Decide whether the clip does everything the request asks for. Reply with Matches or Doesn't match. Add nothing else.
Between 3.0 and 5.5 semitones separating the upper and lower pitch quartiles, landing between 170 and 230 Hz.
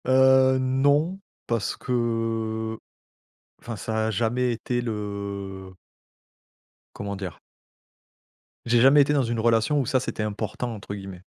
Doesn't match